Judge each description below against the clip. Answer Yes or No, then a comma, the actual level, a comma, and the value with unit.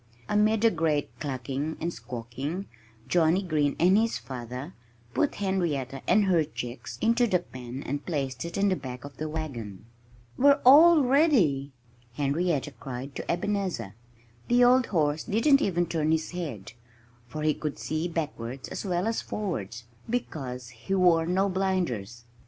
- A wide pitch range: Yes, wide, 6.4 semitones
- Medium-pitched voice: Yes, medium, 160 Hz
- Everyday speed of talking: Yes, average, 150 wpm